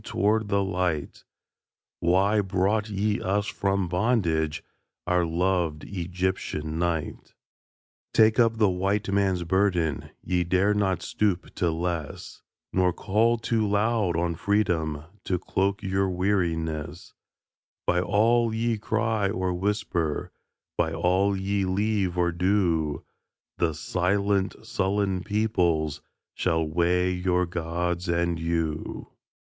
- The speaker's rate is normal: No, slow, 115 wpm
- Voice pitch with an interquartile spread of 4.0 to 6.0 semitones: No, average, 3.0 semitones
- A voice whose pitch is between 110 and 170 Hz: No, very low, 95 Hz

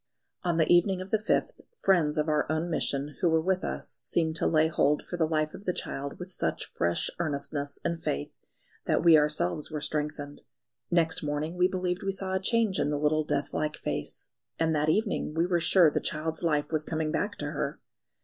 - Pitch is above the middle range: No, medium, 160 Hz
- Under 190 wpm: No, fast, 205 wpm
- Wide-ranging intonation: No, average, 2.9 semitones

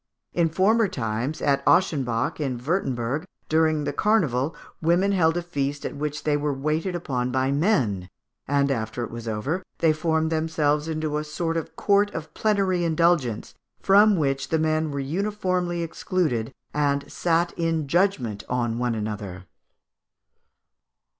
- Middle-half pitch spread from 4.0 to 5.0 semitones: Yes, average, 4.5 semitones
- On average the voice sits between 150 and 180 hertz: Yes, medium, 155 Hz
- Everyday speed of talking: Yes, average, 145 wpm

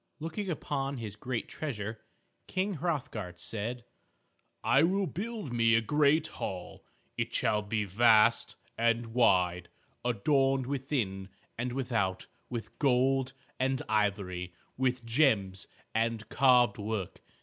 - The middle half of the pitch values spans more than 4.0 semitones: Yes, average, 4.4 semitones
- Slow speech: Yes, slow, 115 wpm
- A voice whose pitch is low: Yes, low, 120 Hz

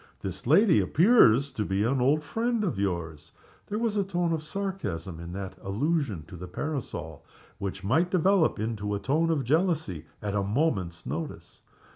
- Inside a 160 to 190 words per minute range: Yes, average, 170 wpm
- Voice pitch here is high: No, low, 135 Hz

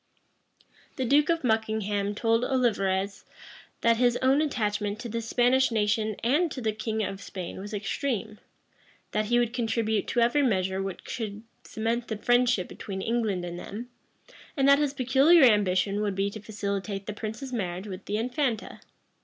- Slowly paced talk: No, average, 165 wpm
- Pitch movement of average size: Yes, average, 3.3 semitones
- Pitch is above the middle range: Yes, high, 220 Hz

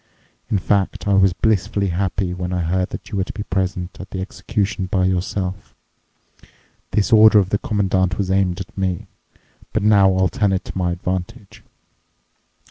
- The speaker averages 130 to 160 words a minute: No, average, 175 wpm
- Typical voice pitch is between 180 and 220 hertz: No, very low, 95 Hz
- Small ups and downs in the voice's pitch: Yes, narrow, 1.6 semitones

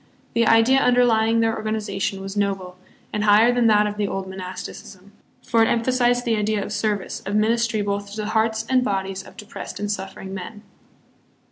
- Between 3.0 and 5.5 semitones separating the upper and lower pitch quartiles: No, narrow, 2.4 semitones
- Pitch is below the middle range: No, high, 210 Hz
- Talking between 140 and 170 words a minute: No, average, 180 wpm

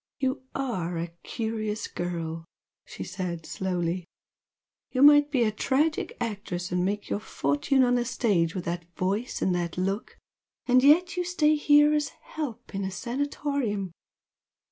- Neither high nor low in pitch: No, high, 215 Hz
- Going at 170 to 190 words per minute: No, average, 150 wpm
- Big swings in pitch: Yes, wide, 7.5 semitones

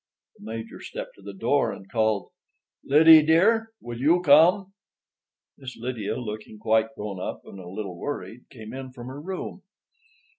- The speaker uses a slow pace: No, average, 160 wpm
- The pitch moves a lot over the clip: Yes, wide, 5.8 semitones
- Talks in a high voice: No, low, 120 Hz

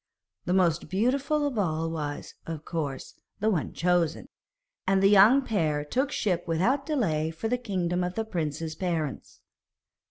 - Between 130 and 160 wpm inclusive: Yes, average, 155 wpm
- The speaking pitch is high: No, medium, 180 Hz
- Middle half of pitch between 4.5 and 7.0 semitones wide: Yes, wide, 5.6 semitones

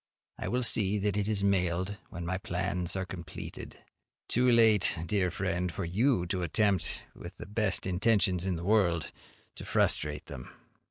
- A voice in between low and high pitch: No, very low, 95 Hz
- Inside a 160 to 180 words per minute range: Yes, average, 165 wpm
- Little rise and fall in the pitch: No, average, 3.0 semitones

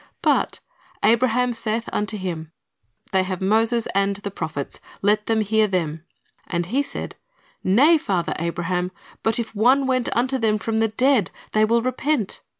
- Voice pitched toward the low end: No, high, 215 Hz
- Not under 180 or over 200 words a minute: No, average, 155 wpm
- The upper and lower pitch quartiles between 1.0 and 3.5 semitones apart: No, average, 4.0 semitones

